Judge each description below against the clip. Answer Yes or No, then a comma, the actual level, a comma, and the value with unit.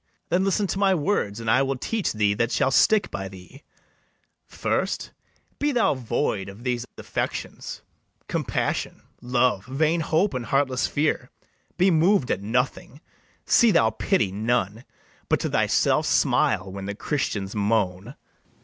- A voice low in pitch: Yes, low, 125 Hz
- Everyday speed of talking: Yes, average, 145 wpm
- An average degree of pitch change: No, wide, 7.8 semitones